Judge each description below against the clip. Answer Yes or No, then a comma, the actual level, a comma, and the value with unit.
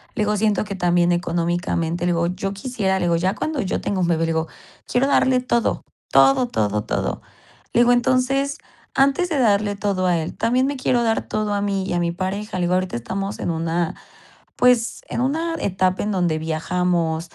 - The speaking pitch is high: Yes, high, 195 Hz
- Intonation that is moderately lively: No, wide, 5.7 semitones